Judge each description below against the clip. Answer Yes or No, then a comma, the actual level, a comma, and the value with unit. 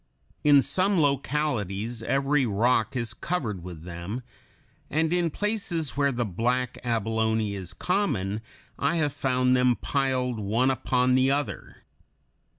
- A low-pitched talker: Yes, low, 125 Hz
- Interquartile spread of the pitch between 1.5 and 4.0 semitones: No, average, 4.6 semitones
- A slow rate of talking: Yes, slow, 130 wpm